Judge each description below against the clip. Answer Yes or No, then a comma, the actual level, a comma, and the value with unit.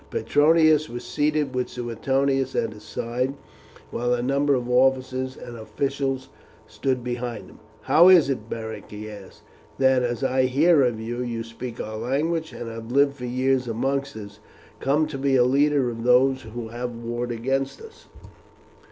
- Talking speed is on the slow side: No, average, 165 wpm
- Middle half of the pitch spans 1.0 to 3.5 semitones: Yes, narrow, 2.6 semitones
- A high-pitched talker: No, low, 130 Hz